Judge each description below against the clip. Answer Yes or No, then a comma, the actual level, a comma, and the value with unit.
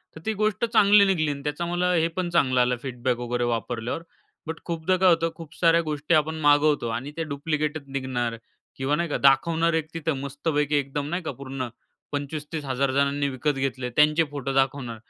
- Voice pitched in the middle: Yes, medium, 145 Hz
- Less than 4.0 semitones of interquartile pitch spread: Yes, average, 3.5 semitones